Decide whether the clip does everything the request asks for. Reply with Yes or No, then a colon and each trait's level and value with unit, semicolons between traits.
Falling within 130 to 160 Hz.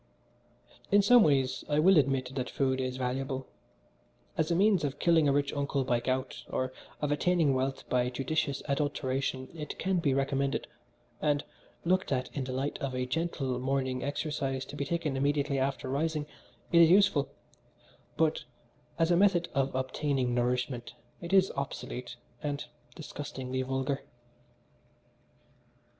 Yes: medium, 140 Hz